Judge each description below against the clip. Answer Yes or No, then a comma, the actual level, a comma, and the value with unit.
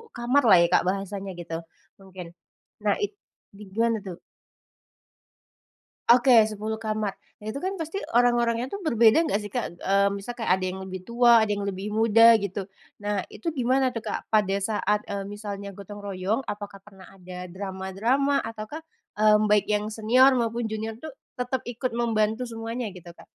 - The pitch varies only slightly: No, average, 3.3 semitones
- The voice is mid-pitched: No, high, 215 Hz